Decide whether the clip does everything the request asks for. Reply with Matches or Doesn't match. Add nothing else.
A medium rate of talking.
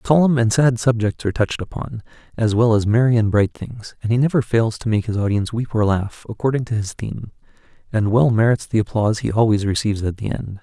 Doesn't match